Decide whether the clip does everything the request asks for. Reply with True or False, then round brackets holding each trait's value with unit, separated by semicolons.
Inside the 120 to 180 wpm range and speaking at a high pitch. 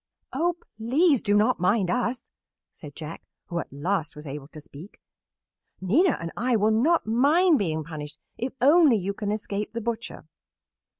True (165 wpm; 210 Hz)